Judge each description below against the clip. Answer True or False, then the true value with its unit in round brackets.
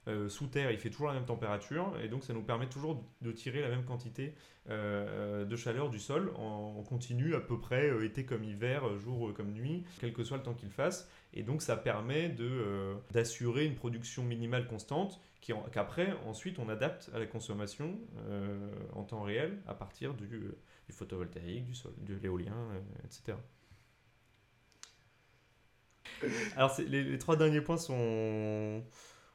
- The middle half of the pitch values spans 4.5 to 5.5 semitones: False (4.0 semitones)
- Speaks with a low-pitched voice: True (115 Hz)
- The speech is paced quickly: False (185 wpm)